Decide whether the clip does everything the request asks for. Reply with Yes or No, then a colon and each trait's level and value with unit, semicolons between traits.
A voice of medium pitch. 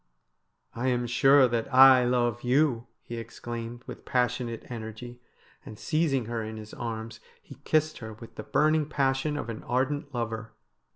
No: low, 120 Hz